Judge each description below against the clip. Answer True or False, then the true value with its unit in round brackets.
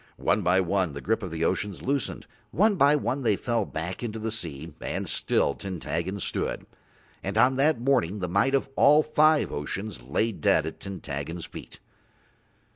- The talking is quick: False (175 wpm)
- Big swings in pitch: True (7.0 semitones)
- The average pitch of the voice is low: True (100 Hz)